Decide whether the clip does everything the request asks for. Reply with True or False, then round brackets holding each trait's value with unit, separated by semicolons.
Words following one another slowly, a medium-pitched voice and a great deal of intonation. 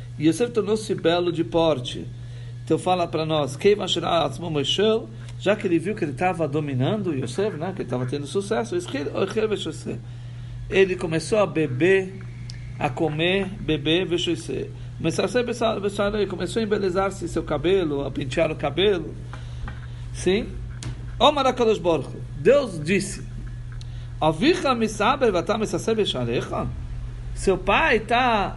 True (110 wpm; 160 Hz; 8.0 semitones)